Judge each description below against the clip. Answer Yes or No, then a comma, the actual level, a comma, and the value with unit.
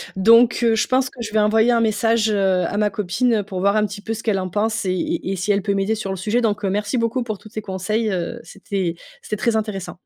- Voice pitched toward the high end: Yes, high, 210 Hz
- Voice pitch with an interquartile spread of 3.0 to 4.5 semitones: No, narrow, 2.5 semitones